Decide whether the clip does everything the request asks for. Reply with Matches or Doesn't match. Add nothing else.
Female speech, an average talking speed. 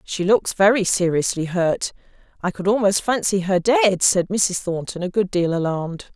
Matches